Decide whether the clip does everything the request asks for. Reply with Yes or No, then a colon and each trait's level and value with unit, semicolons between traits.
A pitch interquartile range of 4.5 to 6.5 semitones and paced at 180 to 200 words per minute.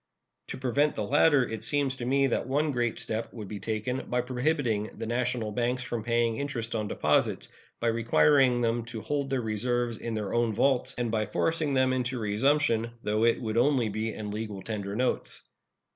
No: average, 2.9 semitones; average, 190 wpm